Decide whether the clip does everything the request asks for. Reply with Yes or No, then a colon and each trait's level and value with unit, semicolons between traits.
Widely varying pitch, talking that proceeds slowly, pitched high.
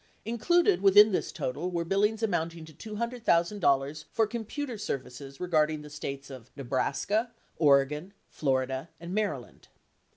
No: wide, 7.1 semitones; slow, 125 wpm; medium, 170 Hz